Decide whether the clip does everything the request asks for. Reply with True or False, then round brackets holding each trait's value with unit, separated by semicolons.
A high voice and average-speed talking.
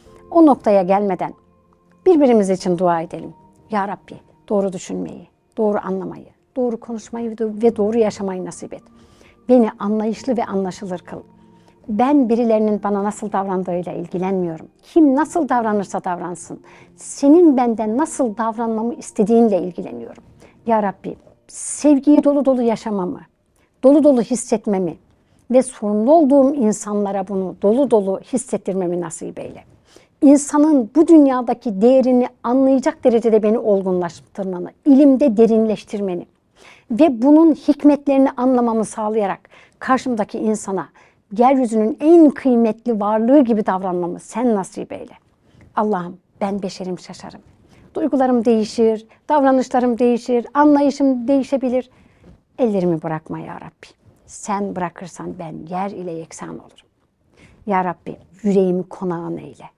True (220 Hz; 110 wpm)